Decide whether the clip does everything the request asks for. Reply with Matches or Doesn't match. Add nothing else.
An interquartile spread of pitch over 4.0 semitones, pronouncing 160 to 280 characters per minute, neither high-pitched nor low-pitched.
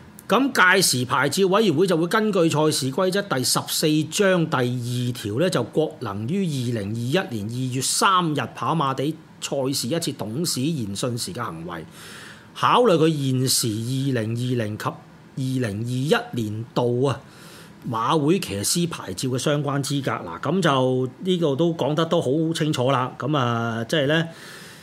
Matches